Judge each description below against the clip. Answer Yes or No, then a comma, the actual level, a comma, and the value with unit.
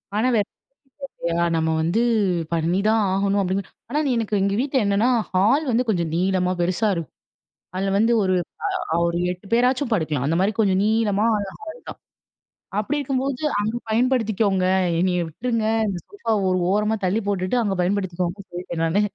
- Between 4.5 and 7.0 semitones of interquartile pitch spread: No, average, 3.8 semitones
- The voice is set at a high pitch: Yes, high, 200 Hz